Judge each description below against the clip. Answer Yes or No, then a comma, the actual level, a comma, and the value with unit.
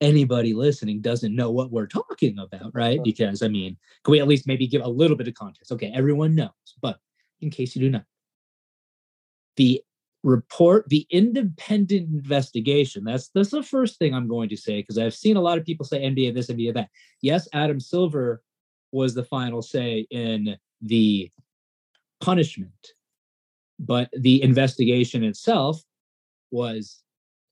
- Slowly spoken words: No, average, 160 wpm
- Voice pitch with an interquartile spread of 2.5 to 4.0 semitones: No, average, 4.8 semitones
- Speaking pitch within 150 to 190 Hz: No, low, 130 Hz